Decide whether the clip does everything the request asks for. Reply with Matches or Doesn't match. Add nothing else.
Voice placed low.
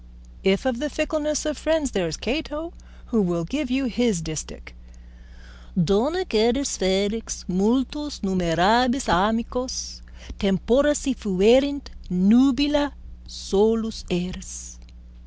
Doesn't match